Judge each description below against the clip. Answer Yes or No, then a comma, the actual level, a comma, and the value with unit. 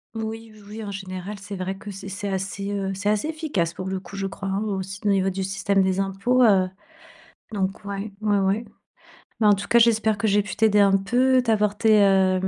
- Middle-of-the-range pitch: No, high, 200 Hz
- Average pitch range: No, narrow, 1.9 semitones